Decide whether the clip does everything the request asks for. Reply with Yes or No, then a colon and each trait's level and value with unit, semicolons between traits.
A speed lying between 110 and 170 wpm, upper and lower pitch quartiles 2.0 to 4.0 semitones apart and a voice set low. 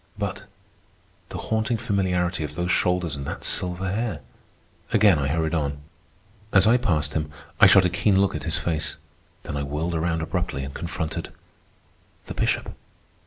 Yes: average, 160 wpm; average, 3.7 semitones; very low, 85 Hz